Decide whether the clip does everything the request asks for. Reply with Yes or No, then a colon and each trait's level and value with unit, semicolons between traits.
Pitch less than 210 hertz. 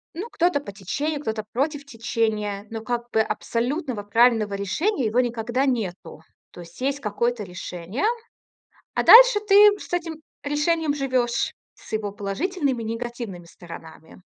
No: high, 240 Hz